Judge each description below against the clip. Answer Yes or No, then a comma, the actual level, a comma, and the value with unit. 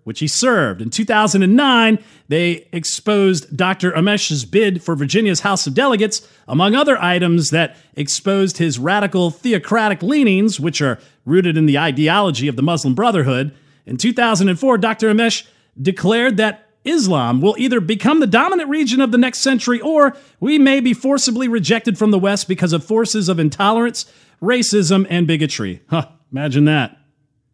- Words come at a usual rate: Yes, average, 155 wpm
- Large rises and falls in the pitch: Yes, wide, 6.6 semitones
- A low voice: No, high, 195 Hz